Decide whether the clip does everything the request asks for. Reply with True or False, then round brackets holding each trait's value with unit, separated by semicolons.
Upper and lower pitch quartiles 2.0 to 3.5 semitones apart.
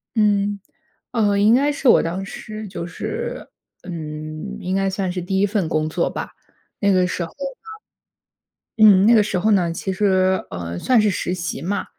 True (3.1 semitones)